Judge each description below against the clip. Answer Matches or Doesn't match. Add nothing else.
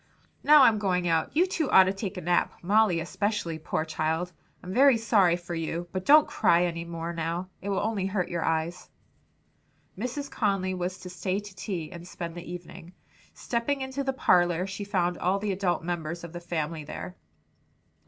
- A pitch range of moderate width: Matches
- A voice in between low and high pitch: Matches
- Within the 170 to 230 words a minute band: Matches